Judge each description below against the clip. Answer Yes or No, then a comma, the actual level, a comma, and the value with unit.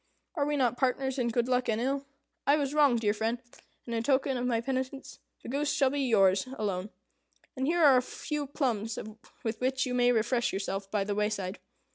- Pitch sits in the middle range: No, very high, 250 Hz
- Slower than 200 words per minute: No, fast, 205 wpm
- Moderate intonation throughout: Yes, average, 3.6 semitones